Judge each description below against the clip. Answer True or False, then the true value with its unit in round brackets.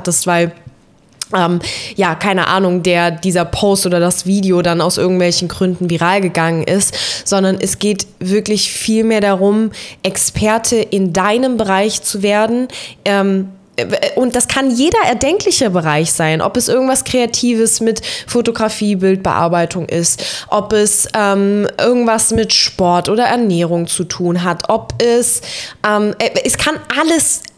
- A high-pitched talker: True (200 Hz)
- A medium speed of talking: True (135 wpm)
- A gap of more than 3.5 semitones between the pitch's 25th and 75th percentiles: True (4.0 semitones)